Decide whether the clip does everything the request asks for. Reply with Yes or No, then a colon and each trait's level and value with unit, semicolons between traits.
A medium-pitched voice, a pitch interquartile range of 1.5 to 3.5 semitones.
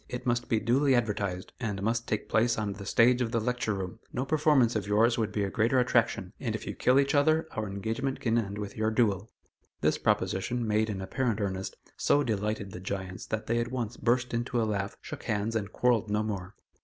No: low, 110 Hz; average, 3.0 semitones